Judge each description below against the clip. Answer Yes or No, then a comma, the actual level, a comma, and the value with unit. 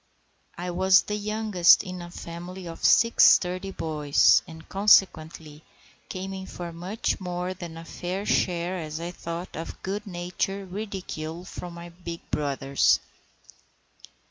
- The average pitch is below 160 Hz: No, medium, 175 Hz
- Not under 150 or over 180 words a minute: No, average, 140 wpm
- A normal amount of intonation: No, narrow, 2.3 semitones